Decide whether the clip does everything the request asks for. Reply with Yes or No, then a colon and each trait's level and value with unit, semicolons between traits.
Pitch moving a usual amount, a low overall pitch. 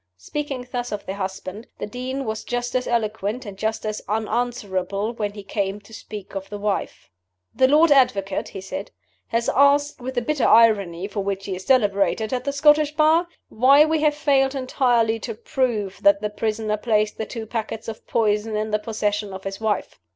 No: average, 3.9 semitones; high, 220 Hz